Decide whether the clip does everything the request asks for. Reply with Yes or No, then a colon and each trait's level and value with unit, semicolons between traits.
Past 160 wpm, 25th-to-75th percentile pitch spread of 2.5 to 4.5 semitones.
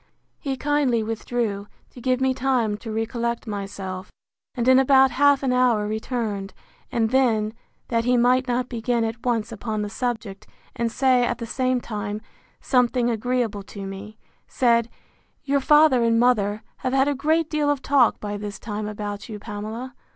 Yes: average, 170 wpm; average, 3.2 semitones